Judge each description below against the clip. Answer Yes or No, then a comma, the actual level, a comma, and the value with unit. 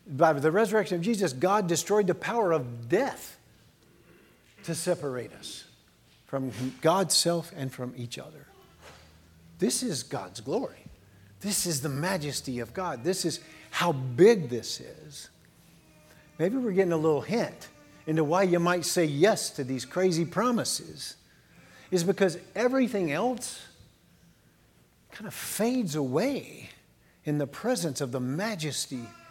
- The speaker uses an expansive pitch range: Yes, wide, 6.1 semitones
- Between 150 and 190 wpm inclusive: No, slow, 135 wpm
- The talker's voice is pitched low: No, medium, 160 Hz